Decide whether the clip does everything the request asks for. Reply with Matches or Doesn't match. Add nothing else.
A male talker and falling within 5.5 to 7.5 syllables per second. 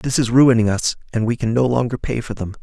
Matches